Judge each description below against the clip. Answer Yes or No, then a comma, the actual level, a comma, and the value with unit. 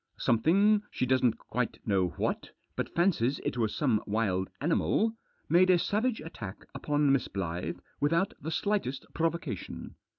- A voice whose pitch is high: No, medium, 140 Hz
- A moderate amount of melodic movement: No, wide, 7.6 semitones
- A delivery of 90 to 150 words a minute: Yes, average, 145 wpm